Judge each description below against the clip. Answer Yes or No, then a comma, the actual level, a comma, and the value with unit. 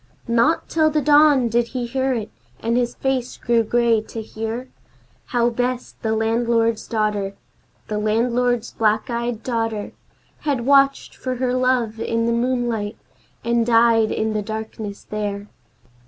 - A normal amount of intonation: No, narrow, 2.1 semitones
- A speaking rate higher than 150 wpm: No, average, 145 wpm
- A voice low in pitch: No, high, 235 Hz